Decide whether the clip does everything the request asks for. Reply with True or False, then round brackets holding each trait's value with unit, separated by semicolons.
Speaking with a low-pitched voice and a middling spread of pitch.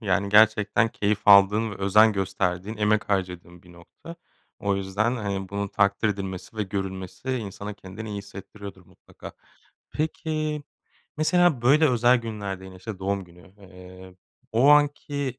True (100 Hz; 3.1 semitones)